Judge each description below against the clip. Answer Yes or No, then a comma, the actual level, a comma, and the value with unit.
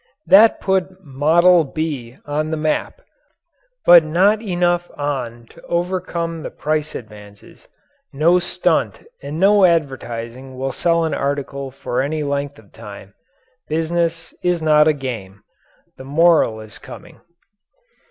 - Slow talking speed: Yes, slow, 130 wpm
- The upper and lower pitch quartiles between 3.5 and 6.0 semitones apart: Yes, average, 4.5 semitones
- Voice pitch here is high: No, medium, 155 Hz